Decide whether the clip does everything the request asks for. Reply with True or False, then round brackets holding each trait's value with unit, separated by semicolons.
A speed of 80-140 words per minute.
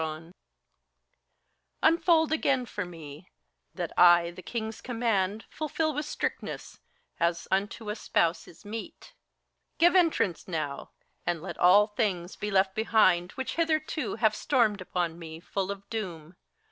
True (135 wpm)